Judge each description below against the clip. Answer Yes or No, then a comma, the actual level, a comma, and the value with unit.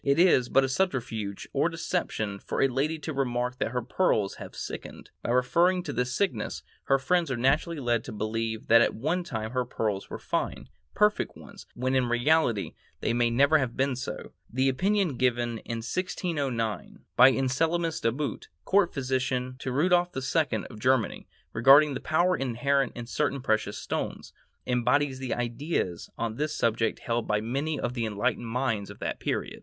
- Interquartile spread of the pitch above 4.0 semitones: Yes, average, 4.4 semitones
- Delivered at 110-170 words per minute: No, average, 180 wpm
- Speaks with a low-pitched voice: Yes, low, 130 Hz